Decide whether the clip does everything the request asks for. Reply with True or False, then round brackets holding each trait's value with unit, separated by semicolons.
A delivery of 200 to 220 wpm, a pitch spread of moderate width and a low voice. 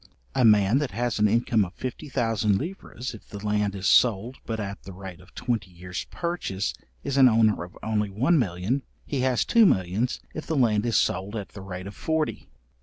True (205 wpm; 4.5 semitones; 110 Hz)